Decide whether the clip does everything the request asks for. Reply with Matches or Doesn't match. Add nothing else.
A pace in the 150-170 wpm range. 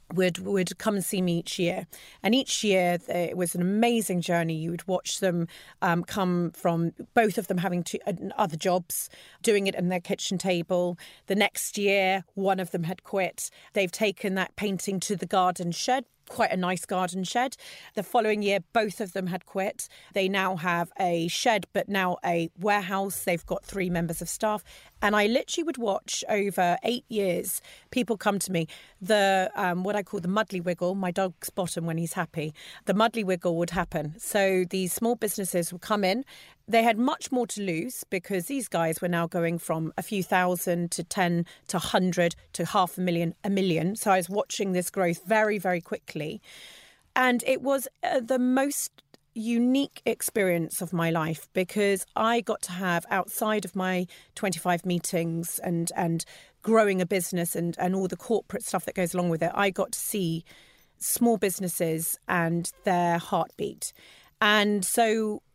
Doesn't match